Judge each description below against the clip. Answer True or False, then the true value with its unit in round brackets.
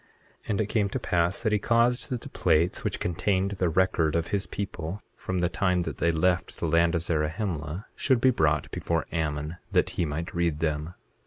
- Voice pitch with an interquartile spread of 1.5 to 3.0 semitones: False (3.6 semitones)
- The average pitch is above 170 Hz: False (85 Hz)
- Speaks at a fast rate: True (210 wpm)